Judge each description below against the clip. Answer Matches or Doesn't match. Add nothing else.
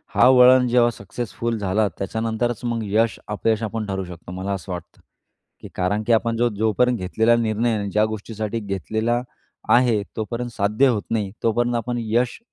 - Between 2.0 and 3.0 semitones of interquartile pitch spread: Matches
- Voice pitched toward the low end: Matches